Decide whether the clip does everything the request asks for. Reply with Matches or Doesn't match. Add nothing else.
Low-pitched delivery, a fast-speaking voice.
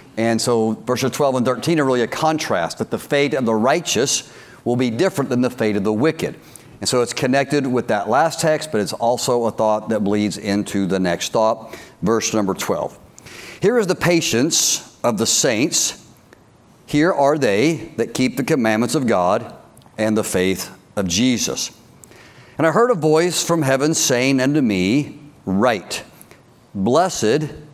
Doesn't match